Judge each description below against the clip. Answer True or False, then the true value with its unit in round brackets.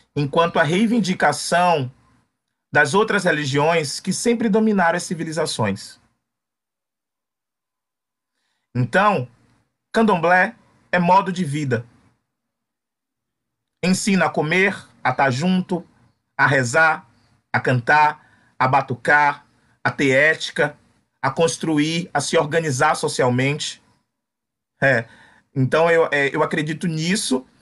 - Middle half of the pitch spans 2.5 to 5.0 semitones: False (5.5 semitones)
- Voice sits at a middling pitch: True (155 Hz)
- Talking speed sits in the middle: False (100 wpm)